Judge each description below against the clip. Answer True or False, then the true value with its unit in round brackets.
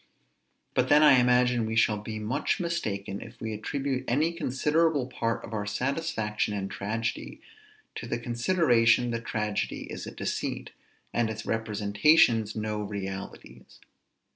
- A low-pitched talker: True (115 Hz)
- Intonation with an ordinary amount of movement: True (3.6 semitones)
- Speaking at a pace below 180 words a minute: True (140 wpm)